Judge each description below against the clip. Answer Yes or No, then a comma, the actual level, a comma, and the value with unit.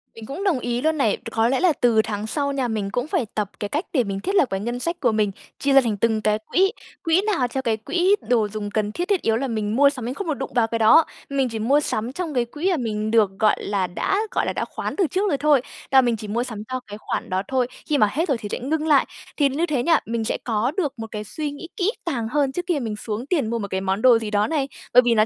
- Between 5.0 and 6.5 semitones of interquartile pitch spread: Yes, average, 5.3 semitones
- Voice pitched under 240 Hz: No, high, 245 Hz